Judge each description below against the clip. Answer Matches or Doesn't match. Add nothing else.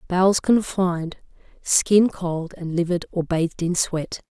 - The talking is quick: Doesn't match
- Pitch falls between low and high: Matches